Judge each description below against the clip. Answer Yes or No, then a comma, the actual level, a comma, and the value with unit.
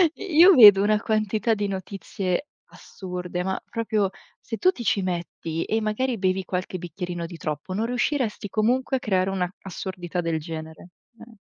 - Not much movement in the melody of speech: No, average, 3.8 semitones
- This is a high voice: Yes, high, 195 Hz